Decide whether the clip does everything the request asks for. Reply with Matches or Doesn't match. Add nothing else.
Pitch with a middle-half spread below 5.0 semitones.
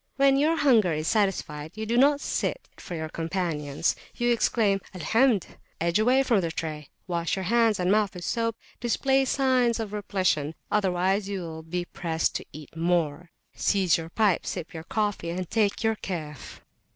Doesn't match